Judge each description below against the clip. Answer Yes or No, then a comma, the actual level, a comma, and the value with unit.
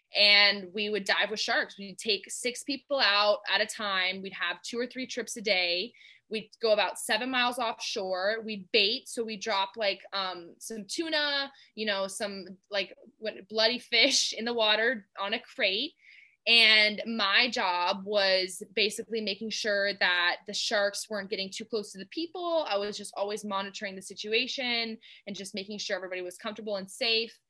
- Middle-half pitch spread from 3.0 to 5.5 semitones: No, narrow, 2.5 semitones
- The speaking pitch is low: No, high, 210 Hz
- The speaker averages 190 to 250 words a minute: No, average, 180 wpm